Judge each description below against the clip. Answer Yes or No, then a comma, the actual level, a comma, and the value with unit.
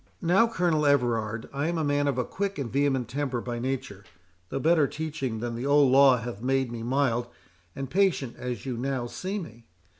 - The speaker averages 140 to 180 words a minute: No, average, 200 wpm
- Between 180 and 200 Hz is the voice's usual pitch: No, low, 135 Hz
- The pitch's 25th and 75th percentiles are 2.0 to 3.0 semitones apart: No, average, 3.4 semitones